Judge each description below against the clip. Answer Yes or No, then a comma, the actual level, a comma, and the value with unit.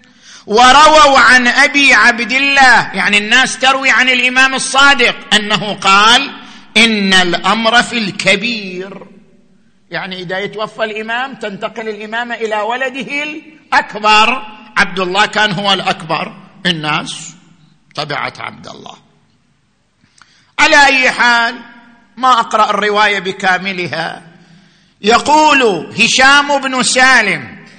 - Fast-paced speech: No, average, 100 wpm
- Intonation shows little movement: No, average, 4.4 semitones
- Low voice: No, high, 220 Hz